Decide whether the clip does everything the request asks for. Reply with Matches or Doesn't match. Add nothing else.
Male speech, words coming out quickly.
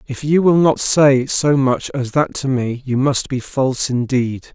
Matches